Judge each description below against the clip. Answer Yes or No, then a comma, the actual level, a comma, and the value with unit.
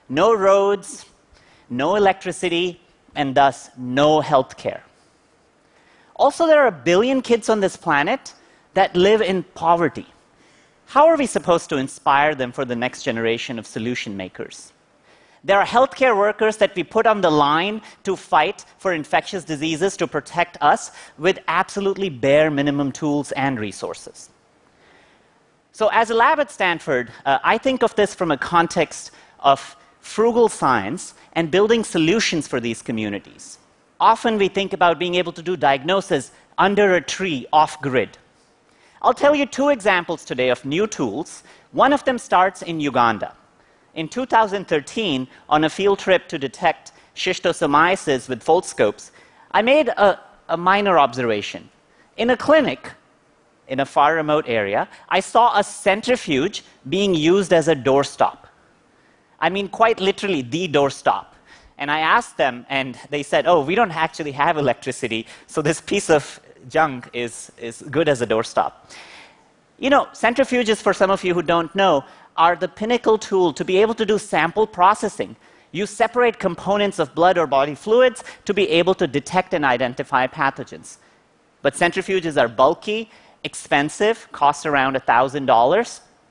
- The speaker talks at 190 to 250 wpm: No, average, 155 wpm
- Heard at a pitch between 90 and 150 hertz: No, medium, 180 Hz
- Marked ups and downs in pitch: Yes, wide, 6.2 semitones